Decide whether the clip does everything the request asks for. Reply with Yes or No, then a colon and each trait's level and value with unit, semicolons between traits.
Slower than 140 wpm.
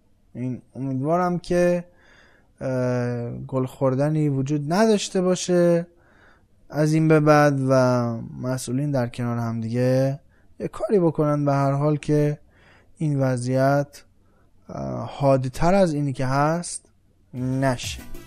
Yes: average, 110 wpm